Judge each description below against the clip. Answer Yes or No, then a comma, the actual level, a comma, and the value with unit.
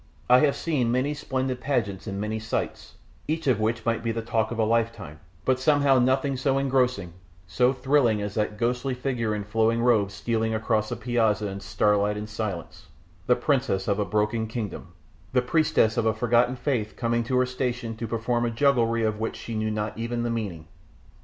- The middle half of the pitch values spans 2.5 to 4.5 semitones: Yes, average, 2.9 semitones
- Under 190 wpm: No, average, 200 wpm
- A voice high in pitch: No, low, 115 Hz